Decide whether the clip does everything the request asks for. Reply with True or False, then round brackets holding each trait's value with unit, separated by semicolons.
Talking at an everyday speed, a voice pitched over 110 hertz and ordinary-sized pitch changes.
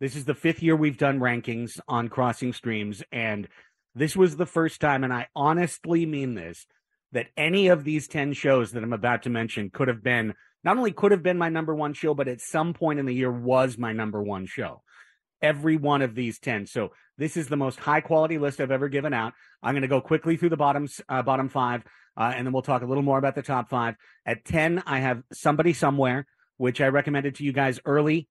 False (235 wpm; 140 Hz; 3.7 semitones)